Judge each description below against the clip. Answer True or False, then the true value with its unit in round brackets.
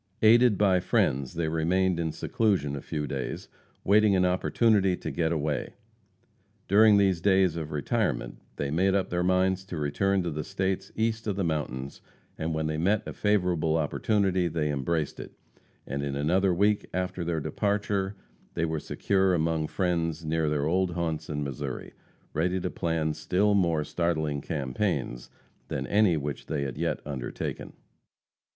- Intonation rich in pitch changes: False (3.8 semitones)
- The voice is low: True (85 Hz)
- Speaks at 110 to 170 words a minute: True (160 wpm)